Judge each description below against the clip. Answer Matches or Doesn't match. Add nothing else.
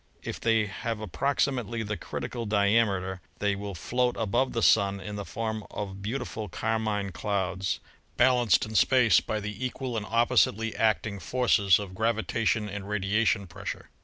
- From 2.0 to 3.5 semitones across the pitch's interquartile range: Matches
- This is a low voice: Matches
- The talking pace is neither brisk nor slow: Matches